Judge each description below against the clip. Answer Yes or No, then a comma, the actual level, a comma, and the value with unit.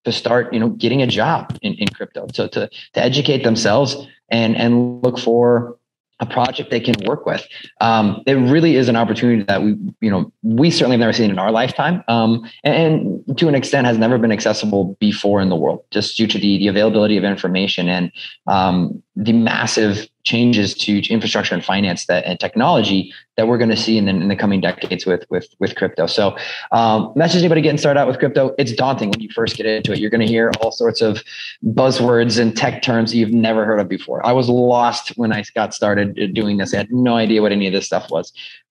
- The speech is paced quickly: Yes, fast, 225 wpm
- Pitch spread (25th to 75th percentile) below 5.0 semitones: Yes, average, 2.8 semitones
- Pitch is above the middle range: No, low, 115 Hz